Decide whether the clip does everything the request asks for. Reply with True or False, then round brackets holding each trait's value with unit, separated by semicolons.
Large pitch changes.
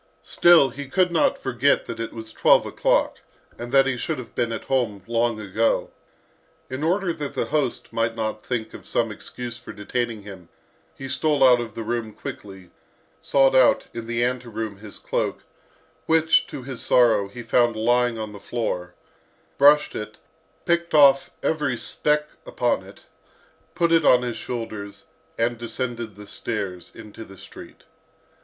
False (3.9 semitones)